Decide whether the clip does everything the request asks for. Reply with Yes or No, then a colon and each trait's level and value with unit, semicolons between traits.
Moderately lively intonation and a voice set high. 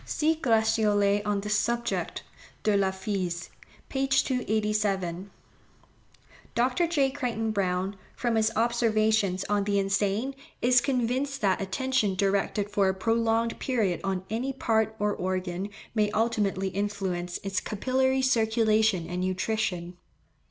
Yes: average, 3.4 semitones; high, 215 Hz